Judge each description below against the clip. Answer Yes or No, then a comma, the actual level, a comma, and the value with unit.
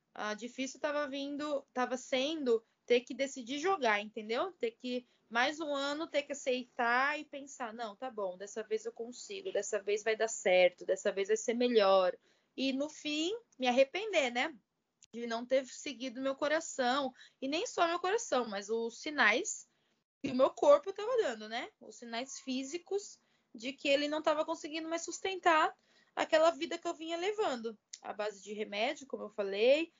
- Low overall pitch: No, very high, 270 Hz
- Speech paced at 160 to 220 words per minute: Yes, average, 180 wpm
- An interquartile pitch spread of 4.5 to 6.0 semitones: Yes, wide, 5.4 semitones